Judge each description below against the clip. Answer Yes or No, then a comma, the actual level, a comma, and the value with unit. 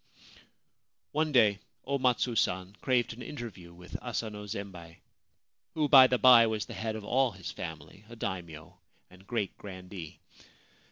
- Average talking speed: Yes, average, 155 wpm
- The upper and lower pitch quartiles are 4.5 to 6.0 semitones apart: Yes, average, 4.9 semitones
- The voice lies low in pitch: Yes, low, 105 Hz